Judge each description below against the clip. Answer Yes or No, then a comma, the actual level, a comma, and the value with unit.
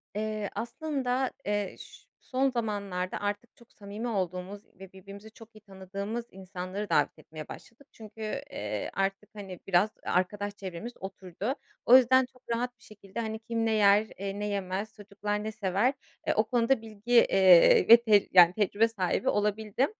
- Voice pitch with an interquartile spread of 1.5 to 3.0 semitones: Yes, average, 2.7 semitones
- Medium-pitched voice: No, high, 210 Hz